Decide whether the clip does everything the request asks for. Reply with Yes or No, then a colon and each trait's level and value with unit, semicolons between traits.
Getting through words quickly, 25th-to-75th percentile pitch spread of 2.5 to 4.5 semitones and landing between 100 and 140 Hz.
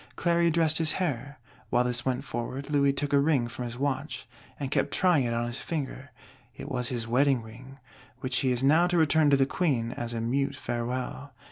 Yes: fast, 210 wpm; average, 3.1 semitones; low, 135 Hz